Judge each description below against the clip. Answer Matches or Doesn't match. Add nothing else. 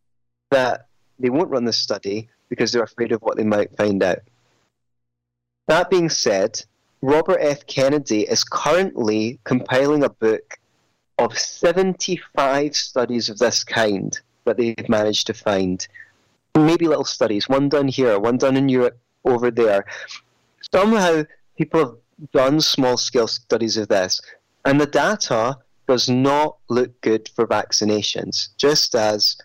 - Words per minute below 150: Matches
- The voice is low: Matches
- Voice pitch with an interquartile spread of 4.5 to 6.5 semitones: Matches